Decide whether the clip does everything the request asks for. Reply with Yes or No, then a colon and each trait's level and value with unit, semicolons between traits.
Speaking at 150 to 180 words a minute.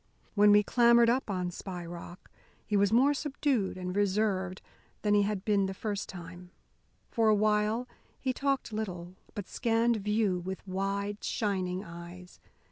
Yes: average, 155 wpm